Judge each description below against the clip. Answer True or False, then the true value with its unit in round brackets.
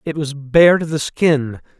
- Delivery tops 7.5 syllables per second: False (3.9 syllables/s)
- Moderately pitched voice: True (145 Hz)